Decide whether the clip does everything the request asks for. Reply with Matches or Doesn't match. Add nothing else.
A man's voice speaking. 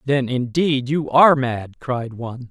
Matches